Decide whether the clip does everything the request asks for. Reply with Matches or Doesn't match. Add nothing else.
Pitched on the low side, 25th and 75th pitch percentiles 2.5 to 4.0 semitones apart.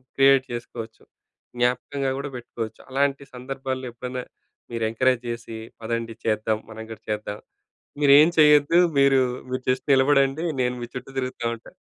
Matches